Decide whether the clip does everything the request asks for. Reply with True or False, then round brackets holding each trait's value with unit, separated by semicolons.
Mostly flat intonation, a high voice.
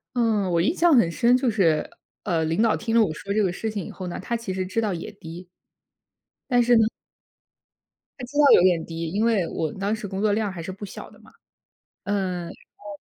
False (4.1 semitones; 200 Hz)